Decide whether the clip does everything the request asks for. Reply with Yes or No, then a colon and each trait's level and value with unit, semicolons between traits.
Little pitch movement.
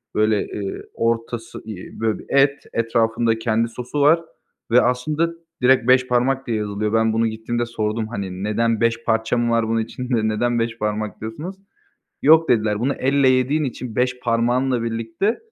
Yes: narrow, 2.3 semitones